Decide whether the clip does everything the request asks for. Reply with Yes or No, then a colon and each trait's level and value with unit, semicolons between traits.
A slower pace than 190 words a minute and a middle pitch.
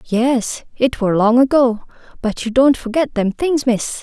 No: average, 180 wpm; high, 245 Hz